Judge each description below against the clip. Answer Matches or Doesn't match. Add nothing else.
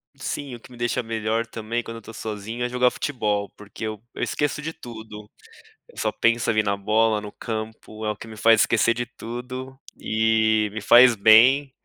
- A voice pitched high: Doesn't match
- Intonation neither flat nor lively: Doesn't match